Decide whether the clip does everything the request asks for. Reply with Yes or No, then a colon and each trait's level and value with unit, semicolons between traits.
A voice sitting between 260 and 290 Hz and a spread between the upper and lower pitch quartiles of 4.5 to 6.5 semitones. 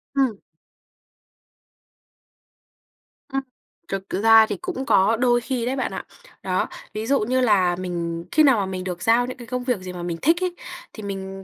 No: high, 225 Hz; average, 5.2 semitones